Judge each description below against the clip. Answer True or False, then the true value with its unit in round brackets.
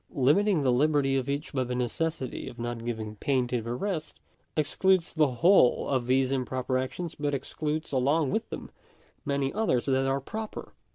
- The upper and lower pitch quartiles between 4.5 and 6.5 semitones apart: False (3.6 semitones)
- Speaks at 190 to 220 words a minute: False (175 wpm)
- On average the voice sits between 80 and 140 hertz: True (135 Hz)